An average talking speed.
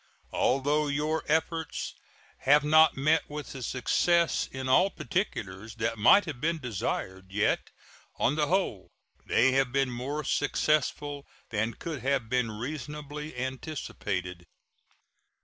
No: slow, 125 wpm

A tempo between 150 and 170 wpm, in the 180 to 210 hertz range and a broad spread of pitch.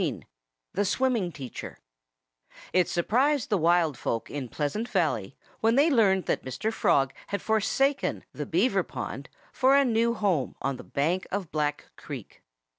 Yes: average, 155 wpm; high, 190 Hz; wide, 7.8 semitones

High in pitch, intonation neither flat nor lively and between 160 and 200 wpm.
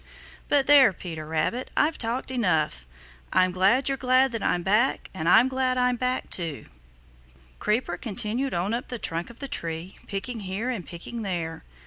No: high, 220 Hz; wide, 6.3 semitones; average, 170 wpm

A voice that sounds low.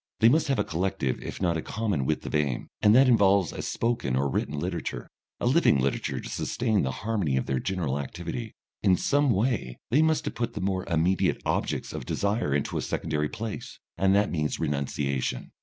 Yes: very low, 95 Hz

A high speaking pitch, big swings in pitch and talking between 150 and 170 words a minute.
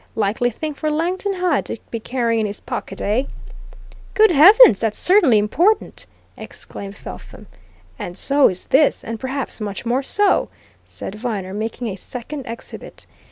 Yes: high, 245 Hz; wide, 6.3 semitones; average, 155 wpm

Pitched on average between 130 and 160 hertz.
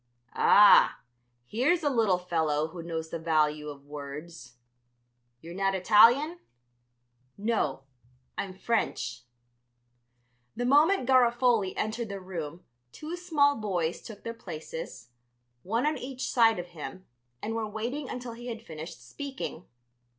No: high, 205 Hz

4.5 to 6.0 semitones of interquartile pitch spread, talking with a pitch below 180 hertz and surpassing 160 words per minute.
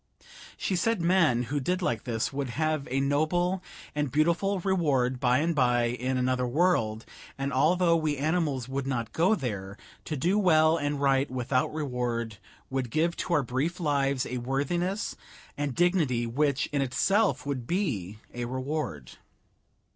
No: average, 5.1 semitones; medium, 140 Hz; average, 155 wpm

